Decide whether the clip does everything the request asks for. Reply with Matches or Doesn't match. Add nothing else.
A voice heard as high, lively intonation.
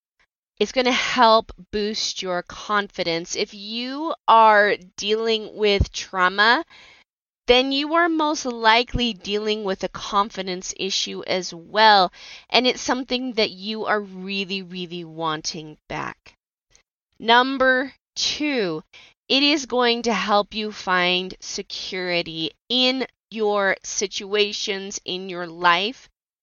Doesn't match